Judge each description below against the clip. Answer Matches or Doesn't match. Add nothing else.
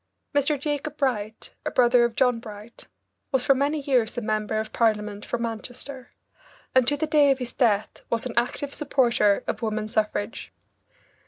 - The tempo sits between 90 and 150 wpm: Doesn't match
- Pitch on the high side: Matches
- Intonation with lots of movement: Doesn't match